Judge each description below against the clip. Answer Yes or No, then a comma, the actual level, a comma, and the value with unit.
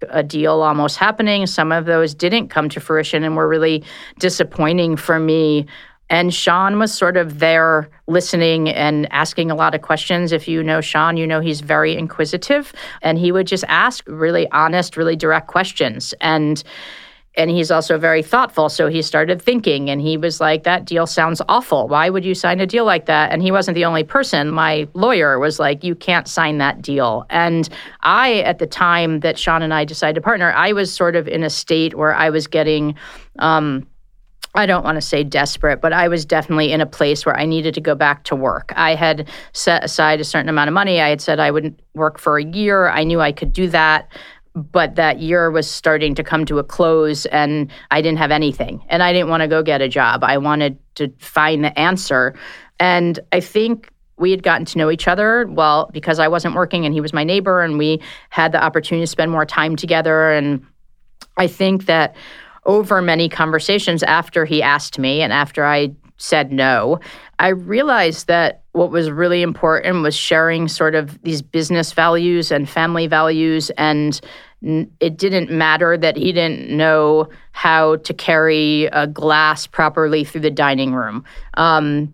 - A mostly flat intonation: Yes, narrow, 2.1 semitones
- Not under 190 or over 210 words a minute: Yes, average, 200 wpm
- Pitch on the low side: No, medium, 160 Hz